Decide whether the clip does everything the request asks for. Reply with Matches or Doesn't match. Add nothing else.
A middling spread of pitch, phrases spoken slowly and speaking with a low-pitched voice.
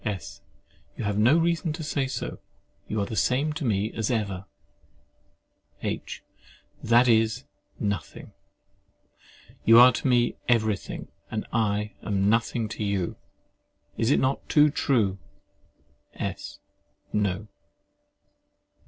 Matches